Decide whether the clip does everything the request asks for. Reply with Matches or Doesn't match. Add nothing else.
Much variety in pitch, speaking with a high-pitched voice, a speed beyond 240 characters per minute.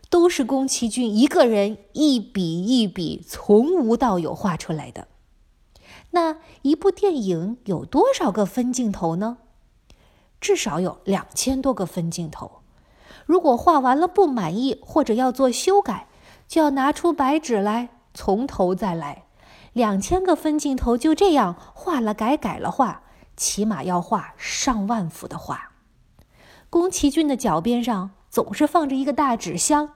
Doesn't match